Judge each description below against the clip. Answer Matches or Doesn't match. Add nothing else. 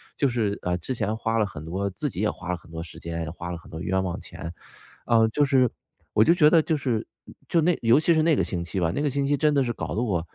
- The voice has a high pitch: Doesn't match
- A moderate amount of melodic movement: Doesn't match